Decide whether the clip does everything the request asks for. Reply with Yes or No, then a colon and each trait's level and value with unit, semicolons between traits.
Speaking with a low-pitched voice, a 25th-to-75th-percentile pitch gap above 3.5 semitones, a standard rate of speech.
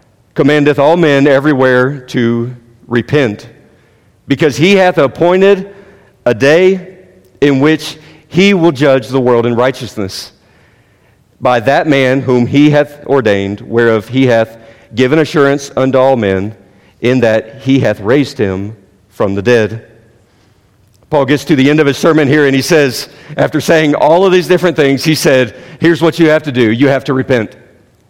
Yes: low, 130 Hz; average, 4.6 semitones; average, 160 wpm